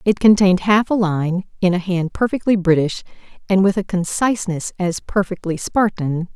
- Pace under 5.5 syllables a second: Yes, 5.0 syllables/s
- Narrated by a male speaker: No, female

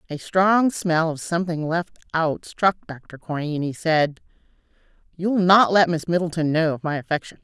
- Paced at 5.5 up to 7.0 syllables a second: No, 4.8 syllables/s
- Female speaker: Yes, female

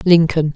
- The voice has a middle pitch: Yes, medium, 165 Hz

